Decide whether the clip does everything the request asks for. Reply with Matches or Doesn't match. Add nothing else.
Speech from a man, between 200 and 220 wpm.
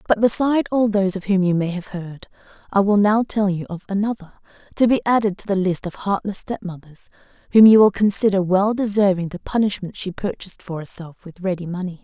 Doesn't match